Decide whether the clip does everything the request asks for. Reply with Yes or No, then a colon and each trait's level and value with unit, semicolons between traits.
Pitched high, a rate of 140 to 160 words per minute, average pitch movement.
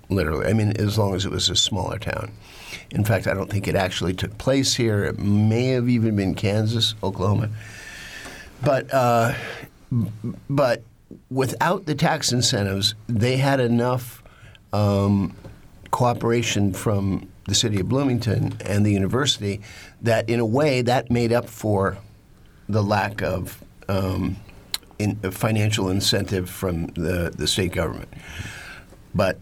No: low, 105 Hz; average, 145 wpm; average, 3.5 semitones